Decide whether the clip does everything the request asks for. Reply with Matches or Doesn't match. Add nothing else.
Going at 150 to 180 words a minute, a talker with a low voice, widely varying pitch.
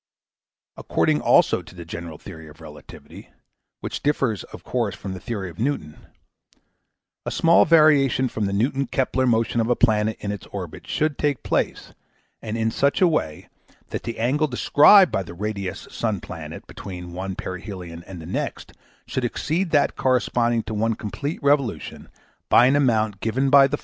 Matches